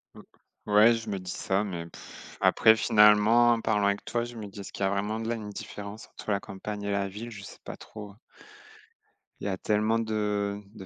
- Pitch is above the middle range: No, low, 105 Hz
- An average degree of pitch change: No, narrow, 1.7 semitones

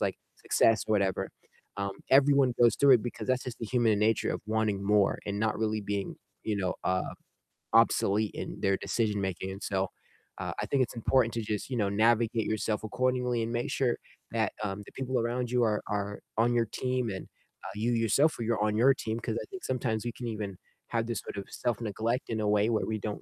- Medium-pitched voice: No, low, 110 Hz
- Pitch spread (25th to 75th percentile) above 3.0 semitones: No, narrow, 2.6 semitones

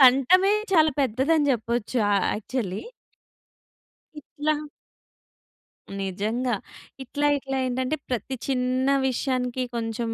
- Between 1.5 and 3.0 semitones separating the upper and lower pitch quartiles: Yes, average, 2.7 semitones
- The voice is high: Yes, very high, 255 Hz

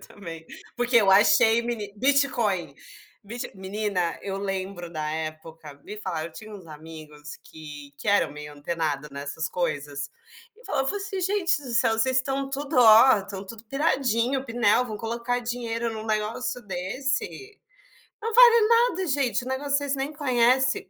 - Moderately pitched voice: No, high, 225 Hz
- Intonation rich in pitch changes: Yes, wide, 7.3 semitones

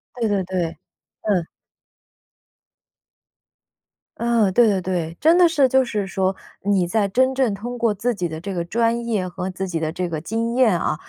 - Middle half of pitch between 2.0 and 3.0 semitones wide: No, average, 4.5 semitones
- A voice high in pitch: Yes, high, 205 Hz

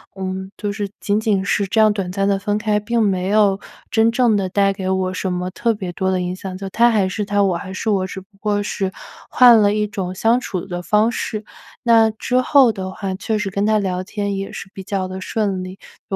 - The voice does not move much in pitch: Yes, narrow, 2.3 semitones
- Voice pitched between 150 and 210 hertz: Yes, high, 200 Hz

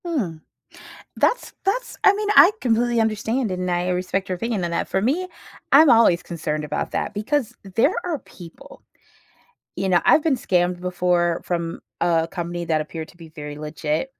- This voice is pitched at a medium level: Yes, medium, 180 Hz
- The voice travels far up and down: Yes, wide, 6.0 semitones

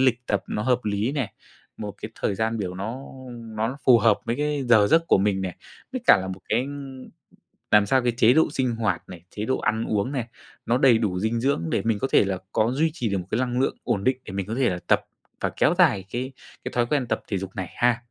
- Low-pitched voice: Yes, low, 115 Hz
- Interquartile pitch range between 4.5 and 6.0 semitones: No, average, 4.1 semitones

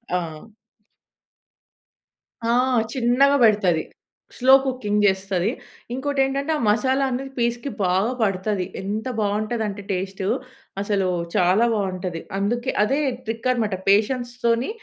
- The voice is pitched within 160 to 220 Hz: Yes, high, 215 Hz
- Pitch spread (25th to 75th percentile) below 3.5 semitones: No, average, 4.2 semitones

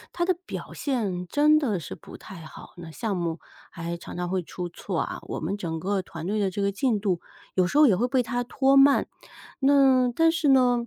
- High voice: Yes, high, 210 Hz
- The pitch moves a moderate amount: No, wide, 7.1 semitones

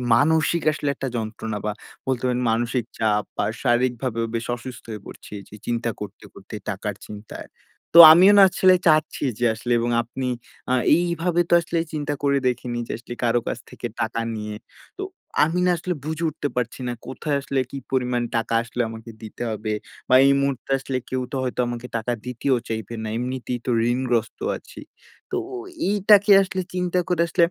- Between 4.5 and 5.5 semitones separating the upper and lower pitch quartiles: Yes, average, 5.1 semitones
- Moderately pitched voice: No, low, 125 Hz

